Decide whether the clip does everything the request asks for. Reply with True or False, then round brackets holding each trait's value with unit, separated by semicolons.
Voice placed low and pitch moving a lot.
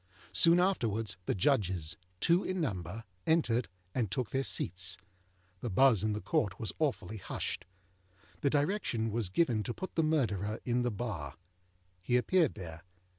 True (115 Hz; 6.5 semitones)